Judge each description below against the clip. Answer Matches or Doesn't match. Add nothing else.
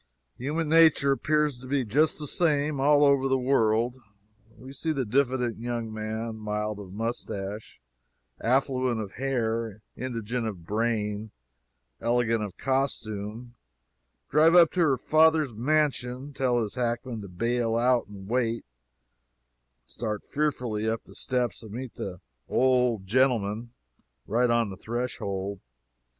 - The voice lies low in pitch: Matches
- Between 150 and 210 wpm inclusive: Doesn't match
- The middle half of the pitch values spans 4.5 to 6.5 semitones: Doesn't match